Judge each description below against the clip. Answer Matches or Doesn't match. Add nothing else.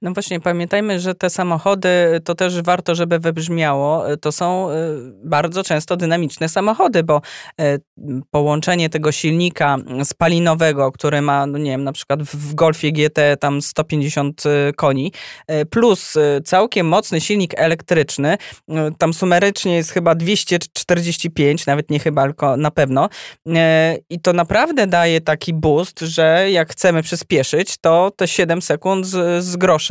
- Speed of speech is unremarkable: Matches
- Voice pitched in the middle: Matches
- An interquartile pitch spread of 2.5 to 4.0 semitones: Matches